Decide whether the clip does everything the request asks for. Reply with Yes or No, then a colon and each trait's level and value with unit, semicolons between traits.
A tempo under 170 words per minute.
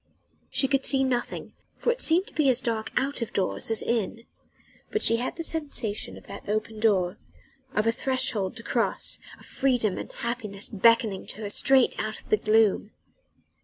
No: average, 185 wpm